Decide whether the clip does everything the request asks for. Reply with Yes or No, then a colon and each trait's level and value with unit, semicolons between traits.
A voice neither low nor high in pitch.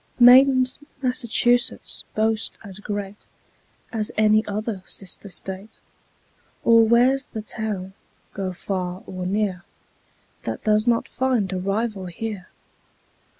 No: high, 215 Hz